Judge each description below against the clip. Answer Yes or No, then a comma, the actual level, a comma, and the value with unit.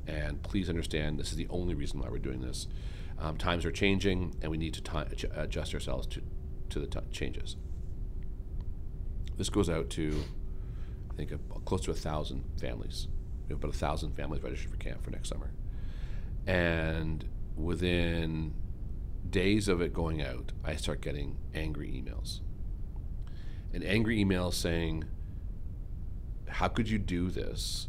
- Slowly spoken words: No, average, 155 wpm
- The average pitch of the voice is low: Yes, very low, 85 Hz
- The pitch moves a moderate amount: Yes, average, 3.4 semitones